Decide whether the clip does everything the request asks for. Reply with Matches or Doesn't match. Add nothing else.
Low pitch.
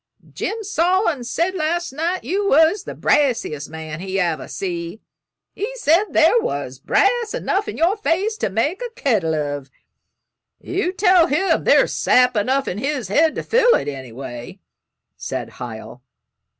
Doesn't match